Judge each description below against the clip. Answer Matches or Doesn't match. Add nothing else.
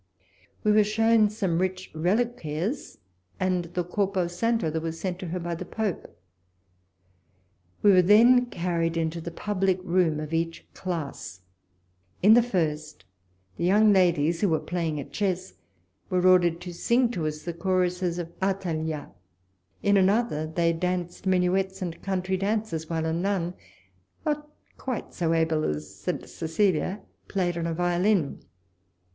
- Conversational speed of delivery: Matches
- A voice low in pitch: Doesn't match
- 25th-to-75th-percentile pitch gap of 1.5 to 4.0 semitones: Matches